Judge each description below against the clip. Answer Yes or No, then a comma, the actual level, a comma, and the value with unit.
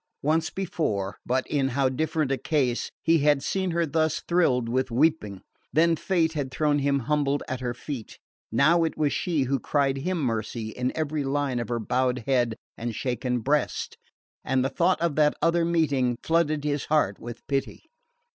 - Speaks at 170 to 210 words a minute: Yes, average, 180 wpm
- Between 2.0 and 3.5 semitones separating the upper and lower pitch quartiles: No, average, 4.0 semitones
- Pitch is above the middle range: No, medium, 140 Hz